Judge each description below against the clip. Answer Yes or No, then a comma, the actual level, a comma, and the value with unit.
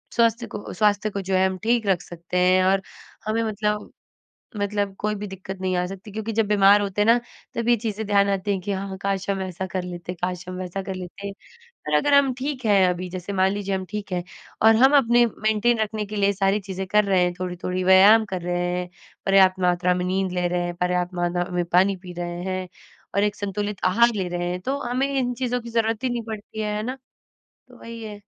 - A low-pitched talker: No, high, 195 Hz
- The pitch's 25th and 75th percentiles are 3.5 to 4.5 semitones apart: No, average, 2.9 semitones